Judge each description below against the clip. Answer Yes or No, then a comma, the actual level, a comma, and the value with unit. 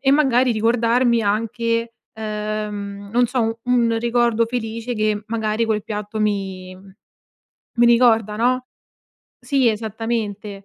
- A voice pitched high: Yes, high, 225 Hz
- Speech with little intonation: Yes, narrow, 2.0 semitones